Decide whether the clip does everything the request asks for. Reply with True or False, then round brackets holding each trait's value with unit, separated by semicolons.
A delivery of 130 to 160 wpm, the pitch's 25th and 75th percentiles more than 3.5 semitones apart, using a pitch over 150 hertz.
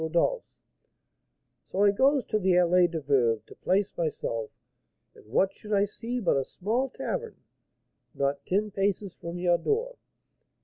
True (150 wpm; 4.2 semitones; 190 Hz)